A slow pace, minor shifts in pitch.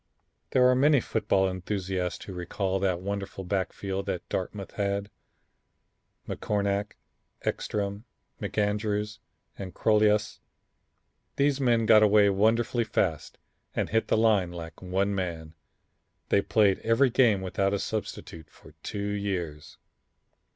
Yes: slow, 120 wpm; narrow, 2.3 semitones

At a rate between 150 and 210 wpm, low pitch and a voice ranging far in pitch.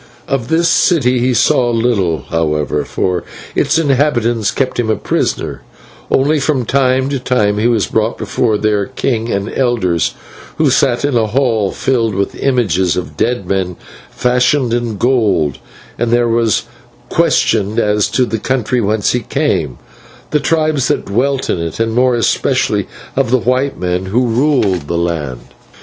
No: average, 160 wpm; low, 115 Hz; average, 4.5 semitones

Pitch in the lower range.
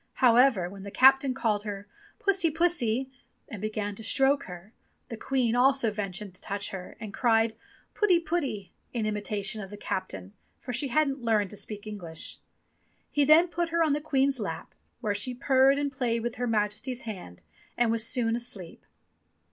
No: high, 230 Hz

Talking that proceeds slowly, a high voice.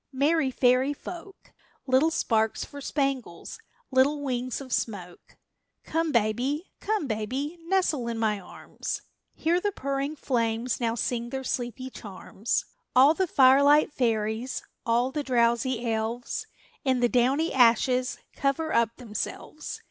Yes: slow, 130 wpm; very high, 255 Hz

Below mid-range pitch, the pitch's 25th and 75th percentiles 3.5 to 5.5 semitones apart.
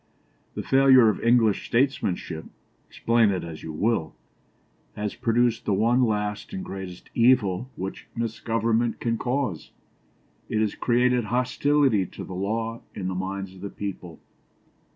Yes: low, 110 Hz; average, 3.9 semitones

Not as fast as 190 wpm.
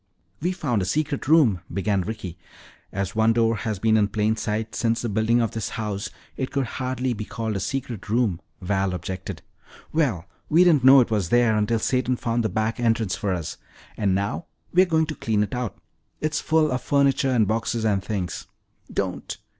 No: average, 195 wpm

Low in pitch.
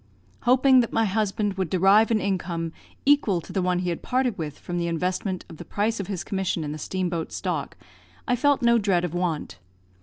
No: high, 190 Hz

